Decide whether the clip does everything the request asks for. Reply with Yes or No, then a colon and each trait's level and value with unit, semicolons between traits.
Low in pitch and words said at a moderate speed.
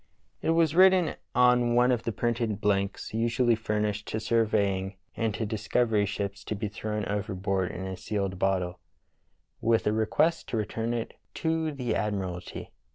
Yes: low, 110 Hz; average, 160 wpm